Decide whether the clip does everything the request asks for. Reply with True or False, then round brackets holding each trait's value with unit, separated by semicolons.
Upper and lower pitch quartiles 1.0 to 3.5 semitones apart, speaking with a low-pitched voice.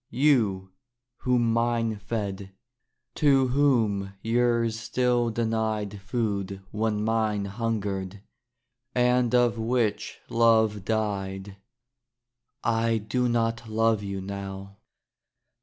True (2.8 semitones; 110 Hz)